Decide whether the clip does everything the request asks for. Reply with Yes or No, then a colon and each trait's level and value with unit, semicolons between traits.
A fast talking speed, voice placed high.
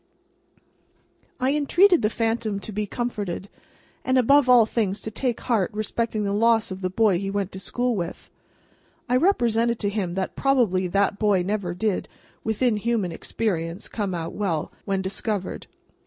No: average, 160 wpm; high, 210 Hz